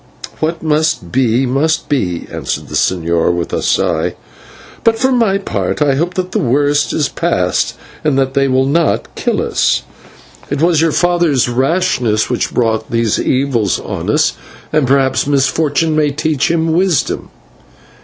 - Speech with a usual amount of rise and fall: Yes, average, 4.1 semitones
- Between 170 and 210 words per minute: No, average, 155 wpm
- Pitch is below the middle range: No, medium, 145 Hz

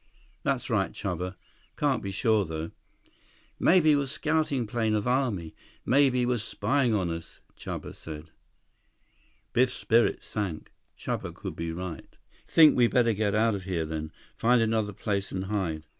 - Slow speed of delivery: No, average, 150 wpm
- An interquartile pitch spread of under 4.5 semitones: No, wide, 5.6 semitones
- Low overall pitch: Yes, low, 110 Hz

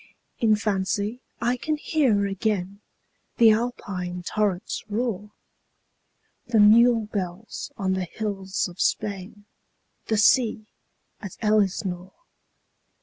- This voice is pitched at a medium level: No, high, 210 Hz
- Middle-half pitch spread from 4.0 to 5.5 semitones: No, average, 2.8 semitones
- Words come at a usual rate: No, slow, 105 wpm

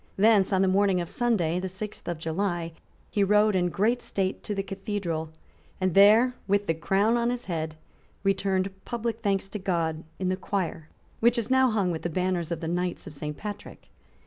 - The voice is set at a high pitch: Yes, high, 195 Hz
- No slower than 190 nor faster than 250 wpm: Yes, average, 200 wpm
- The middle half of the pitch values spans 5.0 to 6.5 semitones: No, average, 3.3 semitones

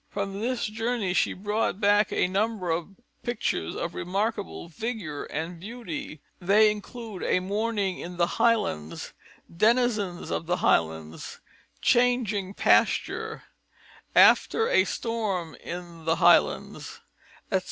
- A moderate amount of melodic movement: Yes, average, 4.5 semitones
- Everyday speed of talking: No, slow, 120 wpm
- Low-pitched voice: No, high, 200 Hz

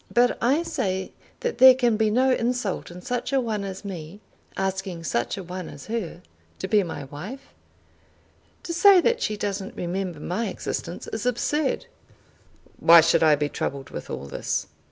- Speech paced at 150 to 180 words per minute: Yes, average, 175 wpm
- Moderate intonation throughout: No, wide, 5.9 semitones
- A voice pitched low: No, high, 200 Hz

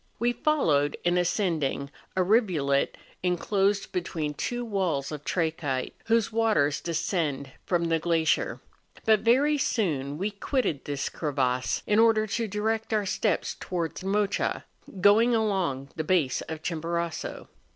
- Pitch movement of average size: No, wide, 6.0 semitones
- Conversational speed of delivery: No, slow, 130 wpm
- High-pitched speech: No, medium, 180 Hz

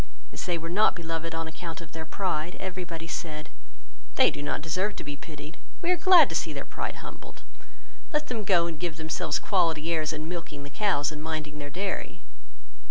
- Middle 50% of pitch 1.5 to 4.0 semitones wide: Yes, average, 2.9 semitones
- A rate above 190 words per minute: Yes, fast, 205 wpm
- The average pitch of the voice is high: No, medium, 165 Hz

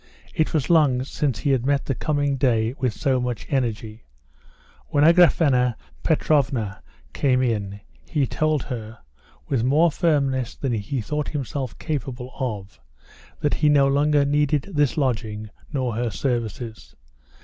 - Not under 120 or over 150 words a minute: Yes, average, 140 wpm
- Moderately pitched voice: No, low, 130 Hz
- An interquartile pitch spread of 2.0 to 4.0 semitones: Yes, average, 3.7 semitones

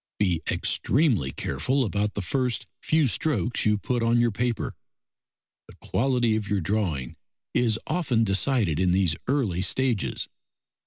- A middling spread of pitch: Yes, average, 4.7 semitones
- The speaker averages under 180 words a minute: Yes, average, 140 wpm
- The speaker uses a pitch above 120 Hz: No, low, 110 Hz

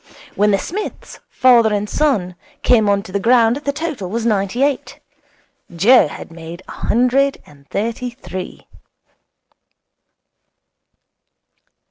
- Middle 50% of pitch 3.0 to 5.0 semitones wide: Yes, average, 4.6 semitones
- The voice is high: Yes, high, 225 Hz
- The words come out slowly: Yes, slow, 120 wpm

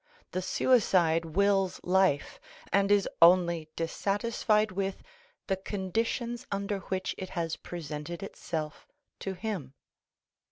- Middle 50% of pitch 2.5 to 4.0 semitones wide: Yes, average, 2.9 semitones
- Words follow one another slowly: Yes, slow, 110 wpm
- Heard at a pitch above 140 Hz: Yes, high, 190 Hz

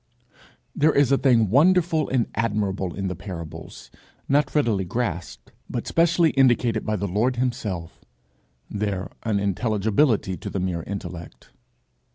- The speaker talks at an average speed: No, slow, 130 wpm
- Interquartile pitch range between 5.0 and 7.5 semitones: Yes, wide, 5.6 semitones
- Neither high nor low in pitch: No, low, 110 Hz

